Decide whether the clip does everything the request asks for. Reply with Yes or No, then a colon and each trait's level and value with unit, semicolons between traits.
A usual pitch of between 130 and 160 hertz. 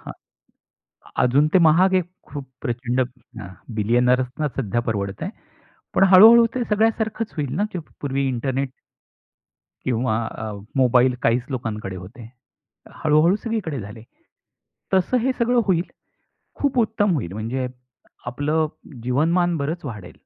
Yes: medium, 140 Hz